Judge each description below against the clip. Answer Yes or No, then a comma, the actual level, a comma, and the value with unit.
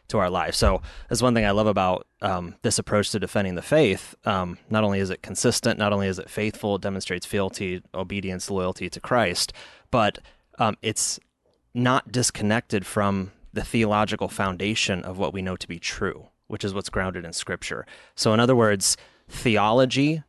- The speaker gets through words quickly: No, average, 185 wpm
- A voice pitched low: Yes, low, 105 Hz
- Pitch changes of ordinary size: Yes, average, 3.0 semitones